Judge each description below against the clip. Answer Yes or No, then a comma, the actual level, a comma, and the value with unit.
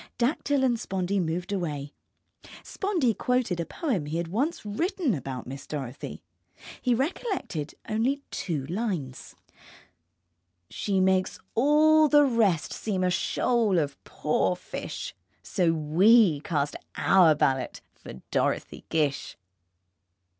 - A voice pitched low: No, high, 190 Hz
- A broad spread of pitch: Yes, wide, 8.0 semitones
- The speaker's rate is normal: No, slow, 120 wpm